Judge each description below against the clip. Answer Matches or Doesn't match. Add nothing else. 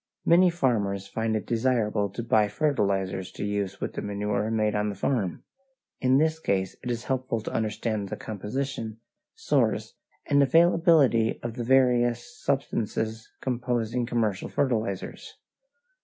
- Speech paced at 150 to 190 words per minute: Doesn't match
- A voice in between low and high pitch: Doesn't match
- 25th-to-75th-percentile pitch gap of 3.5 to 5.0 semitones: Matches